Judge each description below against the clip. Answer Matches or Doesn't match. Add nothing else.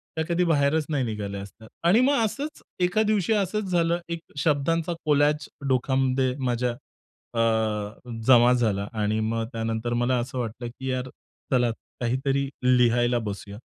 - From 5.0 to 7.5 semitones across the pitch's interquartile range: Matches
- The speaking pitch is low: Matches